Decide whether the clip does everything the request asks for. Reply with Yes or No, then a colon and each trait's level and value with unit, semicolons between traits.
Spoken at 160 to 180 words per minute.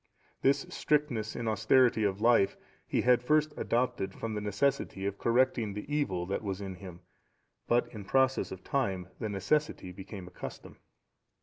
Yes: average, 165 wpm